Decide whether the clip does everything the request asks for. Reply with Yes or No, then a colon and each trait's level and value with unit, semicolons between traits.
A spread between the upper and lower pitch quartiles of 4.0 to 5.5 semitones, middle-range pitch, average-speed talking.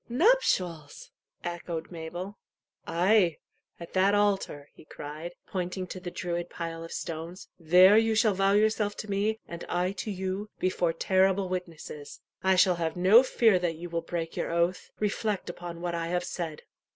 No: average, 2.8 semitones; medium, 180 Hz; average, 165 wpm